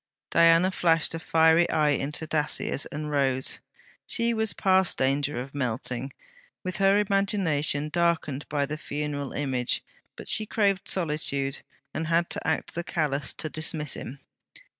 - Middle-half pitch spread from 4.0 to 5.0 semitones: No, average, 3.4 semitones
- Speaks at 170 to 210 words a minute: No, average, 145 wpm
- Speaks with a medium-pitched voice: Yes, medium, 155 Hz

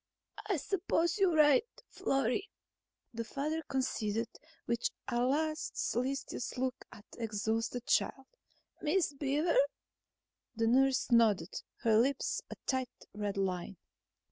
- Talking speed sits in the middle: No, slow, 115 wpm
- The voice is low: No, very high, 260 Hz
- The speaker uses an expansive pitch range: No, average, 4.8 semitones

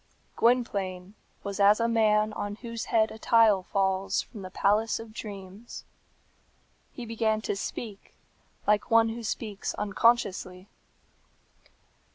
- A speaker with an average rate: No, slow, 125 wpm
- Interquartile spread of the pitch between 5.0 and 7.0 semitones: No, narrow, 2.5 semitones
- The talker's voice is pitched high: Yes, high, 210 Hz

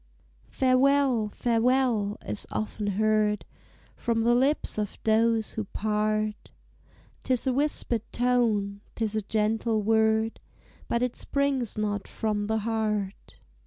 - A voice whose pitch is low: No, high, 220 Hz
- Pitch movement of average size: No, narrow, 2.3 semitones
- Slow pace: Yes, slow, 120 wpm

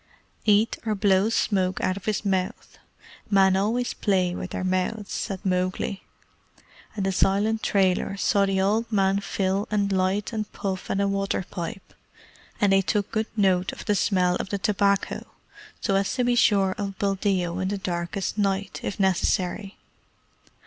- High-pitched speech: Yes, high, 195 Hz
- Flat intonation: Yes, narrow, 1.5 semitones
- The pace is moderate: Yes, average, 165 wpm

